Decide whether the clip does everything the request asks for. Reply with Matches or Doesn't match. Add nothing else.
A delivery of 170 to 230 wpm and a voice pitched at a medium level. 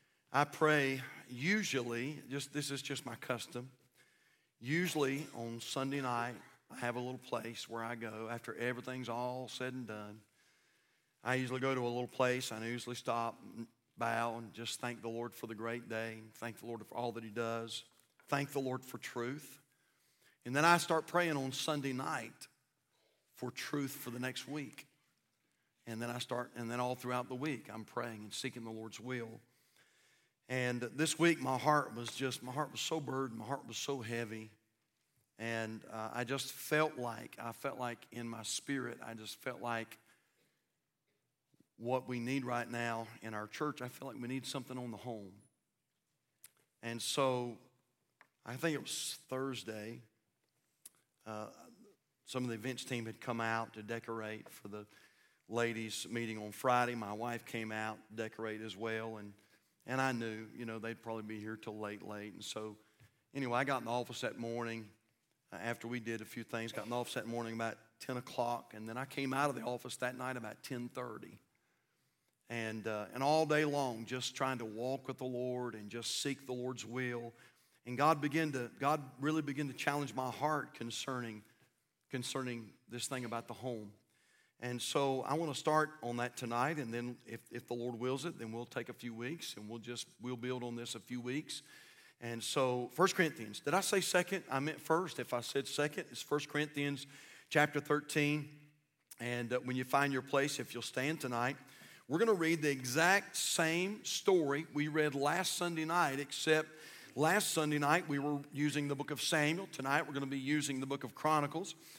Doesn't match